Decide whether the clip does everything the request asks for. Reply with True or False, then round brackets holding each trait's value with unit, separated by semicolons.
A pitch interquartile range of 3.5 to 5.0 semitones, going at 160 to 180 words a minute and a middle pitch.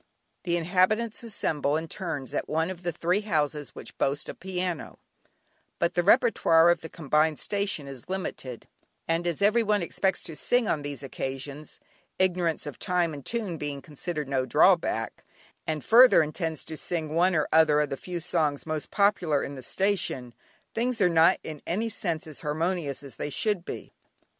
True (3.9 semitones; 175 wpm; 165 Hz)